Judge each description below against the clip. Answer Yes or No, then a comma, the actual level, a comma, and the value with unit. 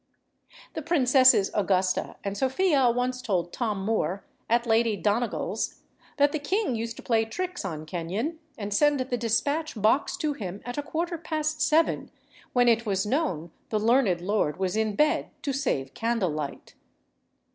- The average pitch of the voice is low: No, high, 235 Hz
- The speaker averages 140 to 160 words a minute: Yes, average, 155 wpm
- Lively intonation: Yes, wide, 6.3 semitones